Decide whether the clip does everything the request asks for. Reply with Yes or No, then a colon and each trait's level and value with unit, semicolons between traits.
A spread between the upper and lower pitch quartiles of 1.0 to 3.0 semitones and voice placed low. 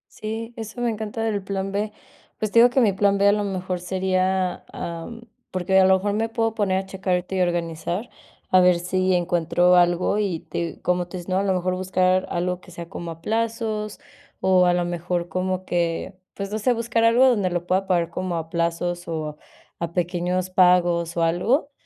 No: average, 2.7 semitones; medium, 185 Hz